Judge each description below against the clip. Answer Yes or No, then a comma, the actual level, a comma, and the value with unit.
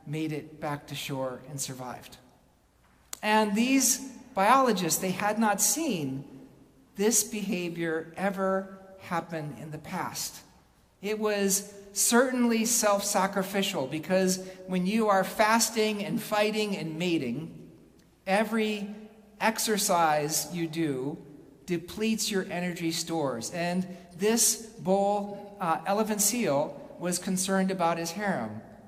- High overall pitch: Yes, high, 195 Hz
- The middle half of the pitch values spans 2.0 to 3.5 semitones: No, average, 4.3 semitones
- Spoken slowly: Yes, slow, 110 wpm